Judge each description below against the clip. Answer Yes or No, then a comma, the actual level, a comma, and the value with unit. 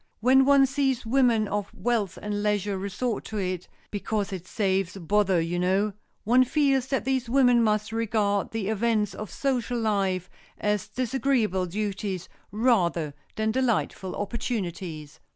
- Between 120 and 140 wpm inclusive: Yes, slow, 135 wpm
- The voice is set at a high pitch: Yes, high, 210 Hz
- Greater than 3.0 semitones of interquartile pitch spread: Yes, average, 4.0 semitones